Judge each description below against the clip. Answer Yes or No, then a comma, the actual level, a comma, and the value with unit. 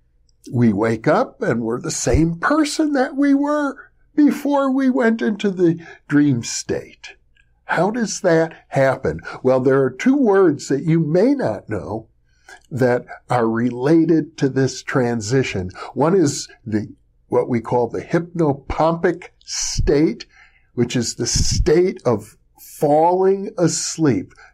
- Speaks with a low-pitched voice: No, medium, 150 Hz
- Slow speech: Yes, slow, 130 wpm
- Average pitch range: No, wide, 7.9 semitones